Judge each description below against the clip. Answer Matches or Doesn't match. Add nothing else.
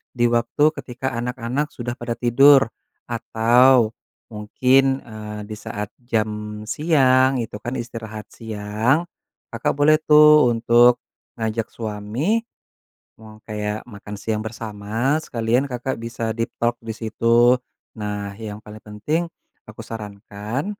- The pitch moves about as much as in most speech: Matches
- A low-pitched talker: Matches